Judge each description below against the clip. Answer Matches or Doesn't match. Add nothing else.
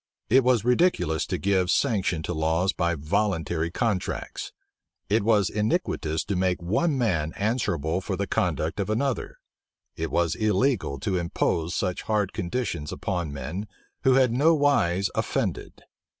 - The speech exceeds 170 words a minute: Doesn't match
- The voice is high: Doesn't match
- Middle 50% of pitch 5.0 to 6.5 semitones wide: Matches